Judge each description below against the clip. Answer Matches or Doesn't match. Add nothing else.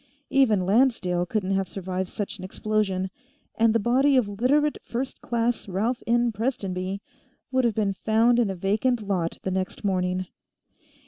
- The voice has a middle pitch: Doesn't match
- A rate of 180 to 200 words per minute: Doesn't match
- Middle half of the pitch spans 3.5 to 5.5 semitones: Matches